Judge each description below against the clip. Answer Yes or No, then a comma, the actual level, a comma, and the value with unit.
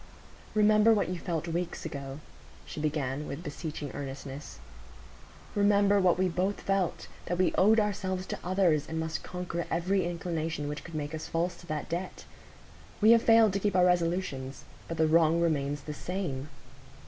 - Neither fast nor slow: Yes, average, 165 wpm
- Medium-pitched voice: Yes, medium, 170 Hz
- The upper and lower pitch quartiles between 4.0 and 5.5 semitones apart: No, average, 3.6 semitones